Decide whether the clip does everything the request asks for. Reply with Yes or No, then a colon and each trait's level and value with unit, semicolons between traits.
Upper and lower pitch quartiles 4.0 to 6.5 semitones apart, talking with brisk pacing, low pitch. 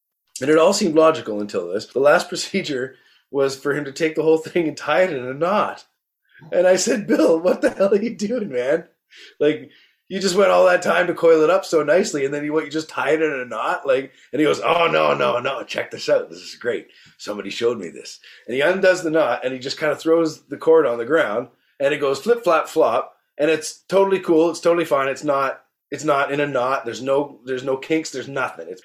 No: average, 5.2 semitones; fast, 250 wpm; medium, 160 Hz